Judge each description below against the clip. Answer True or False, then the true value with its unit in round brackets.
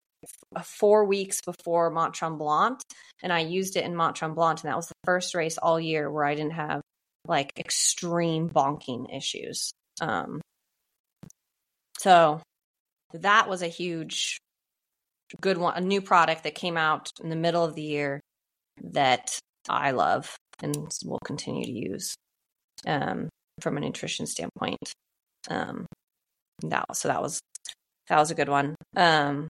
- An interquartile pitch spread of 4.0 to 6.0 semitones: False (2.5 semitones)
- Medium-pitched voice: True (165 Hz)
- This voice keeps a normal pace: True (145 wpm)